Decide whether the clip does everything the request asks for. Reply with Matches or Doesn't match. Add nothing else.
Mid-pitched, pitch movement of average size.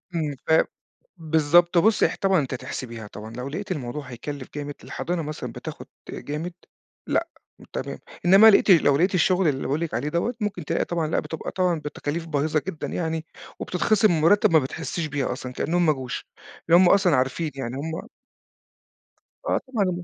Matches